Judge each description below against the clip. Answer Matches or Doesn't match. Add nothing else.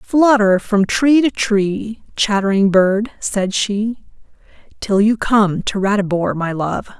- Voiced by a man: Doesn't match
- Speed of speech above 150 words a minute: Doesn't match